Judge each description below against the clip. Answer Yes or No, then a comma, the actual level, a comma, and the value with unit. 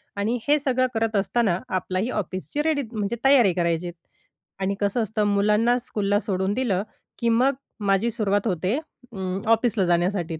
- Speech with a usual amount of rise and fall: Yes, average, 3.8 semitones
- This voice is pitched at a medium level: No, high, 205 Hz